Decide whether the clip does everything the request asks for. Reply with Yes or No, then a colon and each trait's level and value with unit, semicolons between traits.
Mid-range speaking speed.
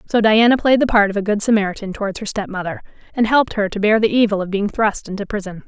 No: fast, 255 wpm